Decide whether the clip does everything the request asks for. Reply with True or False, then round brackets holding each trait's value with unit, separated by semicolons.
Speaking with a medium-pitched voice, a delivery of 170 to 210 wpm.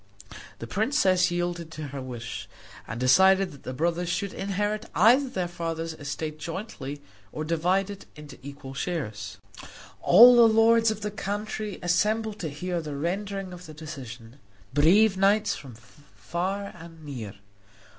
False (175 Hz; 145 wpm)